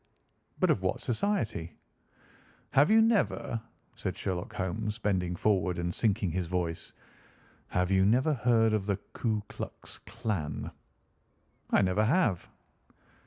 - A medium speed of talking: No, slow, 120 wpm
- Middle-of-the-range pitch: No, low, 105 Hz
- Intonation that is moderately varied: Yes, average, 4.2 semitones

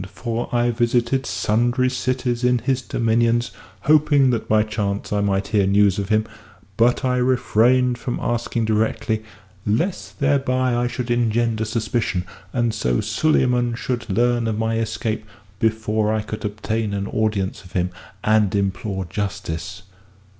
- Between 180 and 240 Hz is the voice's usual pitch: No, low, 115 Hz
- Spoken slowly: No, average, 145 wpm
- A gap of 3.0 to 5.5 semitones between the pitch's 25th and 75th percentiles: No, narrow, 2.6 semitones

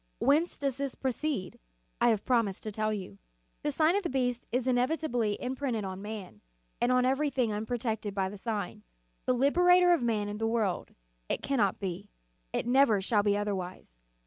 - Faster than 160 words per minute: Yes, average, 180 wpm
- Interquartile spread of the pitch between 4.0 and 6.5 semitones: Yes, average, 4.6 semitones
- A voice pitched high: Yes, high, 235 Hz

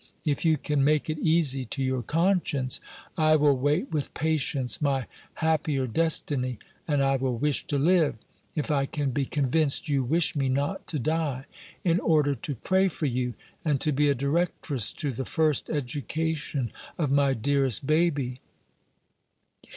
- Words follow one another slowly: No, average, 160 wpm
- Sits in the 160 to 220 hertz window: No, medium, 145 Hz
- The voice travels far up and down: No, average, 2.8 semitones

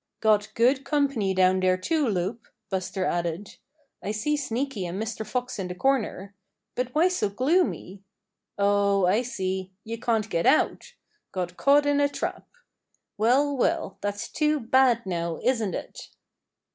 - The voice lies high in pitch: Yes, high, 220 Hz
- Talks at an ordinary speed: Yes, average, 150 wpm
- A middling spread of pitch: No, wide, 5.8 semitones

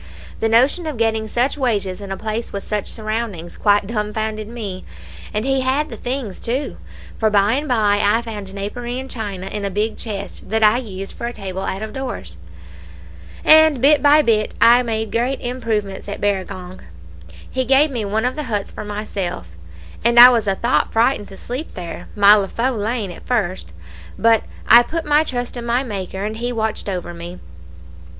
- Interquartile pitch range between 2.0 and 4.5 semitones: Yes, average, 3.4 semitones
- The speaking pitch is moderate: No, high, 220 Hz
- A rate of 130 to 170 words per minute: No, average, 190 wpm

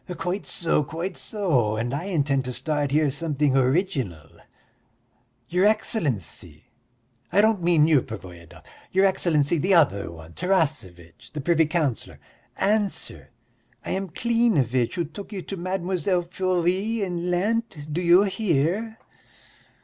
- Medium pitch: Yes, medium, 165 Hz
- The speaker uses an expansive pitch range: Yes, wide, 5.9 semitones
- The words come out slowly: Yes, slow, 130 wpm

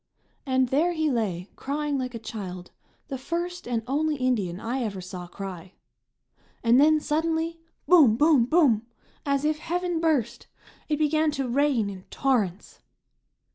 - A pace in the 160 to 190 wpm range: No, average, 145 wpm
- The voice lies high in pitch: Yes, very high, 265 Hz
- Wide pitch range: Yes, wide, 5.9 semitones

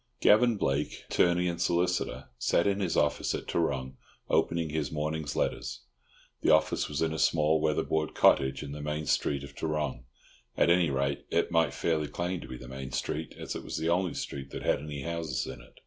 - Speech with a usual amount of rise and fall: Yes, average, 3.3 semitones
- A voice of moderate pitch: No, very low, 75 Hz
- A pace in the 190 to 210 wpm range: Yes, average, 200 wpm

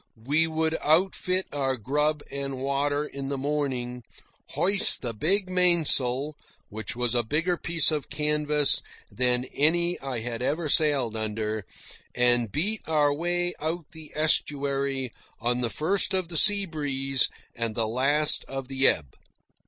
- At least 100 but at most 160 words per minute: Yes, average, 145 wpm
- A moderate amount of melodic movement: Yes, average, 4.2 semitones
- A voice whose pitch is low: No, medium, 145 Hz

